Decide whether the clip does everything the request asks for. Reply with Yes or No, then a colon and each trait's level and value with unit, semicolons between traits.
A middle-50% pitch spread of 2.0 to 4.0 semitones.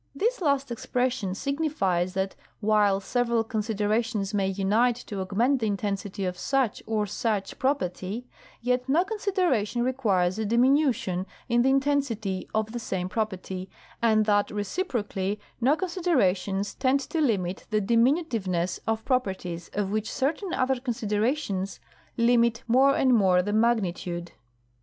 No: average, 4.8 semitones